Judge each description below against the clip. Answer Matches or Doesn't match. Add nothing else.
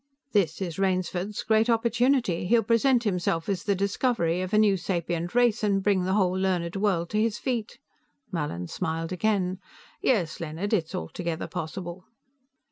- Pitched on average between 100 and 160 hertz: Doesn't match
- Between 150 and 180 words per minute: Matches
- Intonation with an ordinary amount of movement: Matches